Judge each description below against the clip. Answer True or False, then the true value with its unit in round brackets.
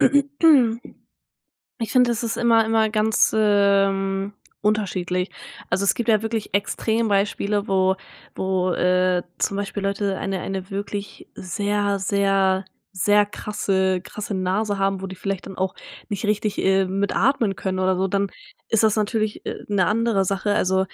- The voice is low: False (200 Hz)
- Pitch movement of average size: False (2.0 semitones)